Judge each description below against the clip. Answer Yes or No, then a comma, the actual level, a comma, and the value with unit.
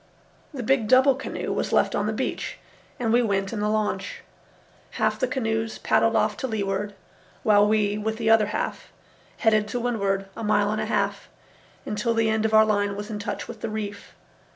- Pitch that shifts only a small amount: Yes, narrow, 1.7 semitones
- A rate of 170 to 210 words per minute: Yes, average, 200 wpm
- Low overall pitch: No, high, 215 Hz